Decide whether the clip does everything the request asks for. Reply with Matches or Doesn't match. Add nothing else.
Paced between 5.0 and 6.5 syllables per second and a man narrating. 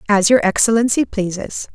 Doesn't match